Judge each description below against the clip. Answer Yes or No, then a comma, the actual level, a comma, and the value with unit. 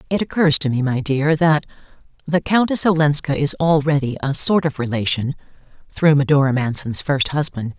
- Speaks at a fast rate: No, average, 155 wpm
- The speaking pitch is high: No, medium, 145 Hz